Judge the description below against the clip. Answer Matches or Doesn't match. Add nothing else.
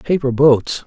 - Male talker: Matches